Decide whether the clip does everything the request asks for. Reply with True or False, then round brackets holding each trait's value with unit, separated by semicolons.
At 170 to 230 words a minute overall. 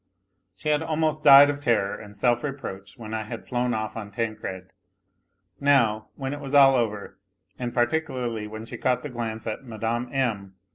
True (180 wpm)